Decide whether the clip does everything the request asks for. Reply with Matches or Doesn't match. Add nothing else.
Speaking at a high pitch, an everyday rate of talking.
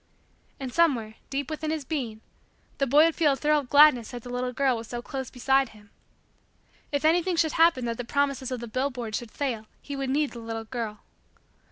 Doesn't match